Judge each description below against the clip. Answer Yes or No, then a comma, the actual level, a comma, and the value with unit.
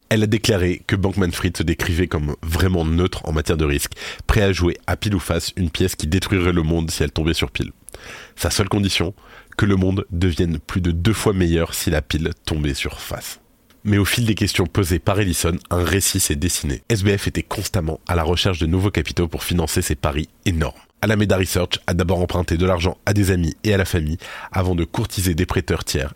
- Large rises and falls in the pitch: No, average, 2.9 semitones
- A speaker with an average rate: No, fast, 225 wpm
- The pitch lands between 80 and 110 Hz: Yes, very low, 90 Hz